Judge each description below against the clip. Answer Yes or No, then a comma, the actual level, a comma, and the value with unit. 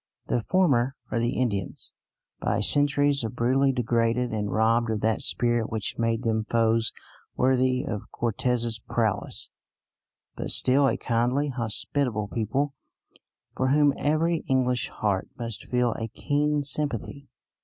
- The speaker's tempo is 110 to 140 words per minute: Yes, slow, 135 wpm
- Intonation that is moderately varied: Yes, average, 3.3 semitones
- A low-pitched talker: Yes, low, 120 Hz